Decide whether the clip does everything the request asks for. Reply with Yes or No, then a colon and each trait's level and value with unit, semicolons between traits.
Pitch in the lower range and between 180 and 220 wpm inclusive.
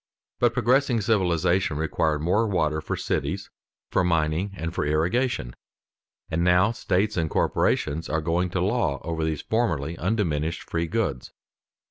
No: very low, 85 Hz; average, 140 wpm